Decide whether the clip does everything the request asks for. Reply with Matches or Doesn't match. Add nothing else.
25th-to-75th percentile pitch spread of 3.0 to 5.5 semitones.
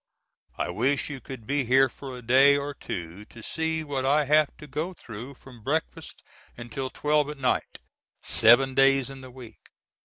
Doesn't match